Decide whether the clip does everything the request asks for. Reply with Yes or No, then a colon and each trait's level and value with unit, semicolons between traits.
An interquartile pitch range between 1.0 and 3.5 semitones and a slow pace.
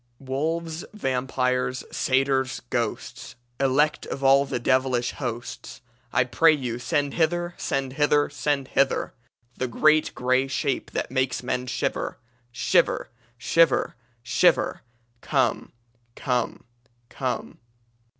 Yes: narrow, 2.5 semitones; slow, 110 wpm